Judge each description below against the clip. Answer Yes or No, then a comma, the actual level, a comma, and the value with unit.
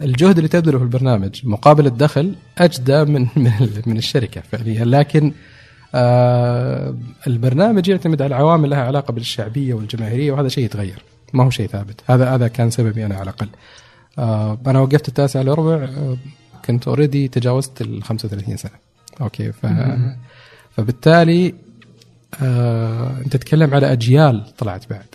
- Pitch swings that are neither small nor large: Yes, average, 3.8 semitones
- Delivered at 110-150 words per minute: Yes, average, 130 wpm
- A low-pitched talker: Yes, low, 125 Hz